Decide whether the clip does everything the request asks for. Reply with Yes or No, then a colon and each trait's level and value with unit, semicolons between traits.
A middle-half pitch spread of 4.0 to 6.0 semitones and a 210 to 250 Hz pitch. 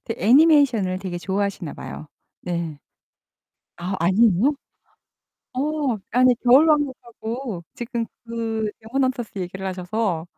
Yes: average, 5.2 semitones; high, 220 Hz